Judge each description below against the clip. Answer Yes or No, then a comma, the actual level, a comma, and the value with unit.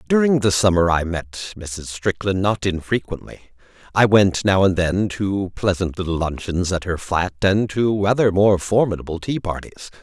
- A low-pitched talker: Yes, very low, 95 Hz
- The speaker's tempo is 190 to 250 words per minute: No, average, 170 wpm